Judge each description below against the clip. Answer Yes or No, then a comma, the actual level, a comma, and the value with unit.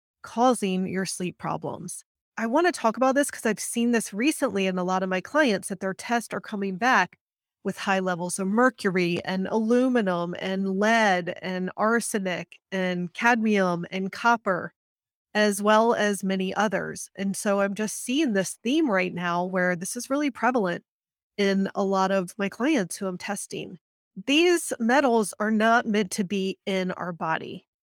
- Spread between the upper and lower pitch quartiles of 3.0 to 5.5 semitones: Yes, average, 3.7 semitones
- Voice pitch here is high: Yes, high, 200 Hz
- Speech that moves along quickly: No, average, 175 wpm